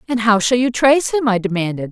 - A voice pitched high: Yes, high, 225 Hz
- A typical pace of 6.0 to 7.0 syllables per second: Yes, 6.4 syllables/s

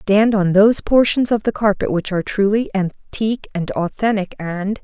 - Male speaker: No, female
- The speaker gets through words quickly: No, average, 160 wpm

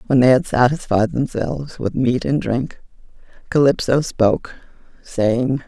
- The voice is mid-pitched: No, low, 125 Hz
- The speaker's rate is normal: No, slow, 125 wpm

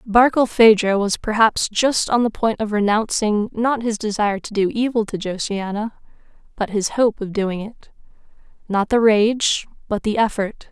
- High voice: Yes, high, 215 Hz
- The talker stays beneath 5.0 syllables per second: Yes, 4.6 syllables/s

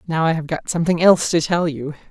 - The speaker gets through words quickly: Yes, fast, 255 wpm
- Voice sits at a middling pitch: Yes, medium, 165 Hz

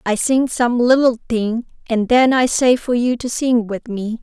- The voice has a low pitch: No, high, 240 Hz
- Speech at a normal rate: No, fast, 215 wpm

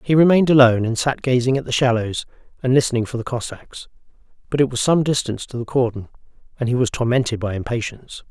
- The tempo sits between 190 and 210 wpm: Yes, average, 200 wpm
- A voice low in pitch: Yes, low, 125 Hz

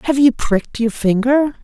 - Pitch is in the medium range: No, very high, 250 Hz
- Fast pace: No, average, 185 wpm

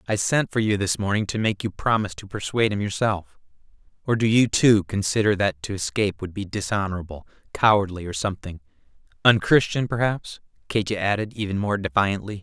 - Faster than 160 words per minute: Yes, average, 170 wpm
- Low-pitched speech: Yes, low, 105 Hz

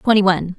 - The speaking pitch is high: Yes, high, 195 Hz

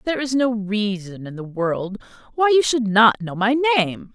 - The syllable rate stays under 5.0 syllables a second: Yes, 4.7 syllables/s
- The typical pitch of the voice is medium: No, high, 225 Hz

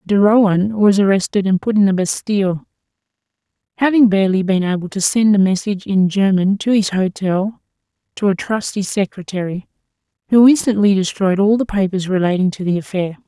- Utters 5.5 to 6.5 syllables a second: Yes, 5.6 syllables/s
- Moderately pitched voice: No, high, 195 Hz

